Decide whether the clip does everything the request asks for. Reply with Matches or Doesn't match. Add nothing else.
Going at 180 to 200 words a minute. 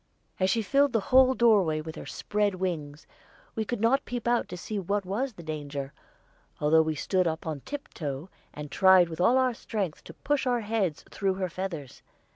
Matches